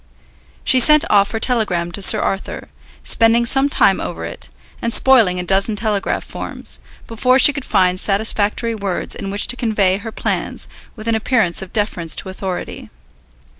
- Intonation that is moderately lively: Yes, average, 3.4 semitones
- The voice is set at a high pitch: Yes, high, 215 Hz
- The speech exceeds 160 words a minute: Yes, average, 170 wpm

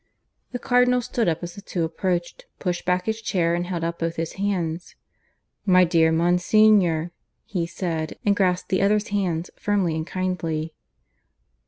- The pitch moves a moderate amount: Yes, average, 3.2 semitones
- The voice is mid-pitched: Yes, medium, 180 Hz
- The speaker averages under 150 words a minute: No, average, 160 wpm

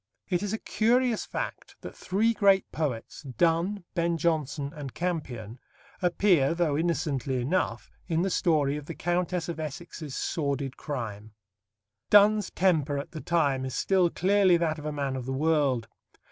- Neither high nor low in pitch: Yes, medium, 160 Hz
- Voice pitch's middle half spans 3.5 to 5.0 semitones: Yes, average, 4.5 semitones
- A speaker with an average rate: Yes, average, 160 wpm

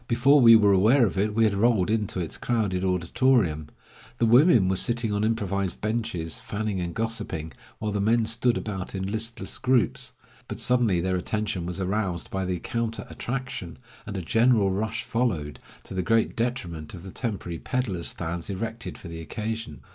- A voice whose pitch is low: Yes, low, 105 Hz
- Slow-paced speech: No, average, 175 wpm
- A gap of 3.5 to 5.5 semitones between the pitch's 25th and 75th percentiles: Yes, average, 3.9 semitones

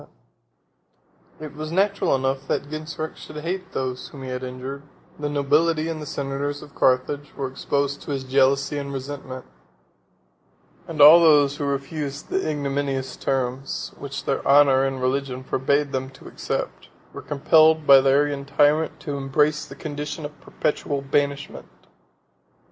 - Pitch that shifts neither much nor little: No, narrow, 1.8 semitones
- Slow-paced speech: No, average, 150 wpm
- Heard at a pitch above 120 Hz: Yes, medium, 140 Hz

